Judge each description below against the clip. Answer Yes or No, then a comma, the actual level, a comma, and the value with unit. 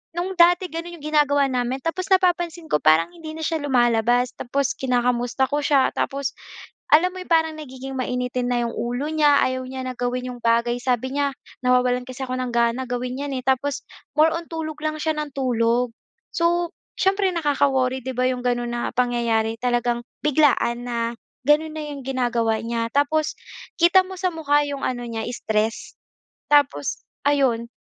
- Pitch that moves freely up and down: No, average, 4.0 semitones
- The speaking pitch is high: Yes, very high, 260 Hz